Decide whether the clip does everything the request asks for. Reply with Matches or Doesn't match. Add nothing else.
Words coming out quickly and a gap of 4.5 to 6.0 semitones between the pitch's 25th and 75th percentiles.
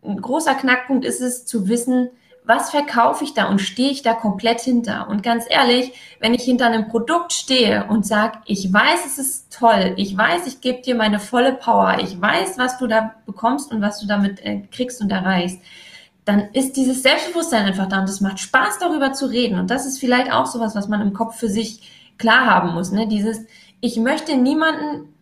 Doesn't match